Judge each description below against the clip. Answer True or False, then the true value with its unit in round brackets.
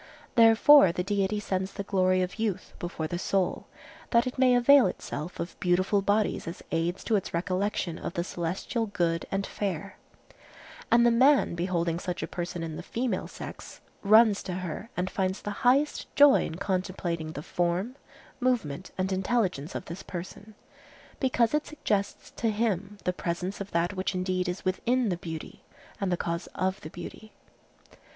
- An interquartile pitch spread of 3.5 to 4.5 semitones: True (3.9 semitones)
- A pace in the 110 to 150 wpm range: False (170 wpm)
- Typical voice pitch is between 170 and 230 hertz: True (190 Hz)